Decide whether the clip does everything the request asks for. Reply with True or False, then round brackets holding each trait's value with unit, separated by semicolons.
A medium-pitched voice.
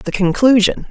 False (215 Hz)